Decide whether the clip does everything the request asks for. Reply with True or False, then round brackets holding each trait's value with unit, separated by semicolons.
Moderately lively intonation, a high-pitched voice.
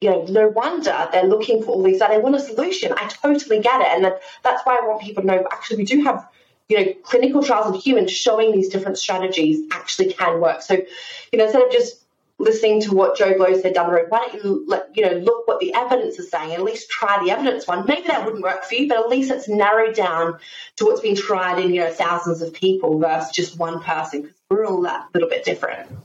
False (7.2 semitones; 215 Hz)